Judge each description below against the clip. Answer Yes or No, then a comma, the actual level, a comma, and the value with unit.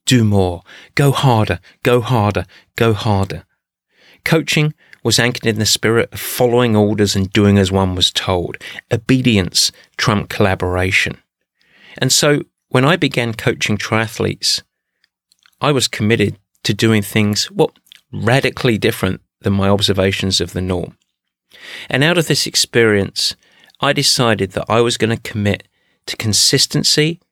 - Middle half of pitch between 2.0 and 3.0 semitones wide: No, average, 4.4 semitones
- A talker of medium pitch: No, low, 110 Hz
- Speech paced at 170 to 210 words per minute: No, average, 140 wpm